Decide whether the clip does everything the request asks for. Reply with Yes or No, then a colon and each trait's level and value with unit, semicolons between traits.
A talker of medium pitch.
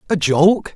Yes: medium, 170 Hz